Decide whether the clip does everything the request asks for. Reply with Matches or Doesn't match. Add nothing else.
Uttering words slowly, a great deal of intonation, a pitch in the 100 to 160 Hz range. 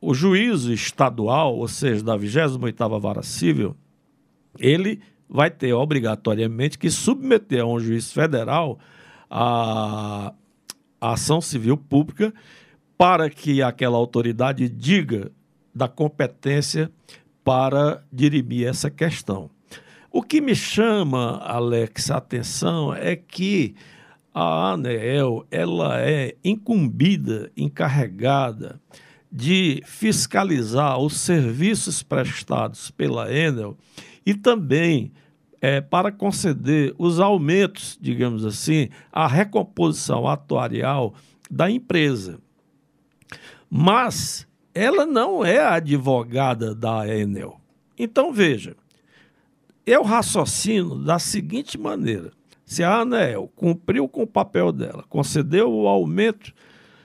Matches